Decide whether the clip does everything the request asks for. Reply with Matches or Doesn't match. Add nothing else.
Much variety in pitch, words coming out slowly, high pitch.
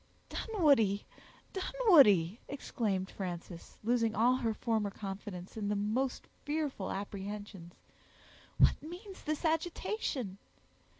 Matches